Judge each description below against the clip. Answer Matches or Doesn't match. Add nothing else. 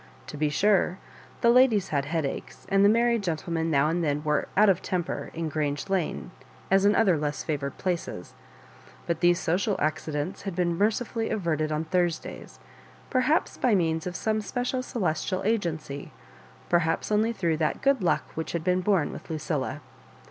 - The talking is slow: Doesn't match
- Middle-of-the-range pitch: Matches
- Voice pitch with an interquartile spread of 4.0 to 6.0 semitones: Matches